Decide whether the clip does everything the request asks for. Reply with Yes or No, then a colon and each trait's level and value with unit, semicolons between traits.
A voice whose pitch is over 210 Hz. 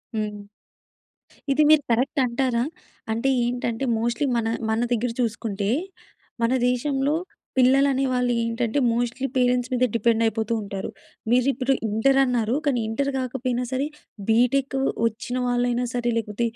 Yes: high, 245 Hz